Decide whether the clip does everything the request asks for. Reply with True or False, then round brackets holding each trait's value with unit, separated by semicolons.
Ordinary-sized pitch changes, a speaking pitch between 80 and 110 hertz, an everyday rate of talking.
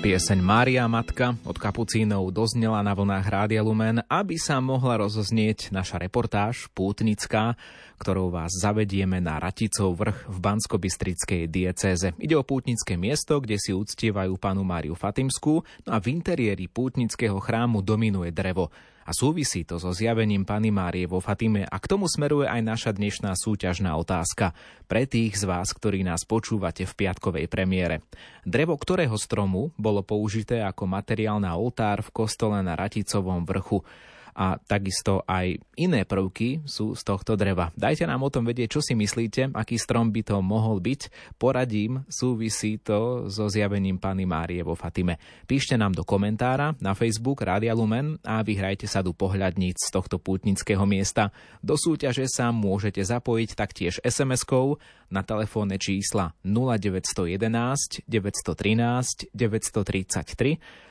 True (3.5 semitones; 105 Hz; 145 wpm)